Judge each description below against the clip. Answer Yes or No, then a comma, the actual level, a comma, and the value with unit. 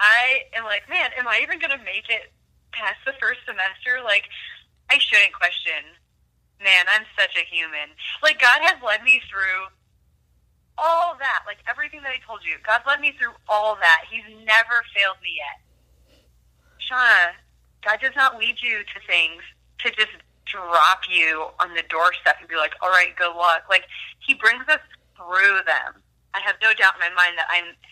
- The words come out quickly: No, average, 185 wpm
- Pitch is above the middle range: Yes, high, 205 Hz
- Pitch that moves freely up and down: Yes, wide, 6.6 semitones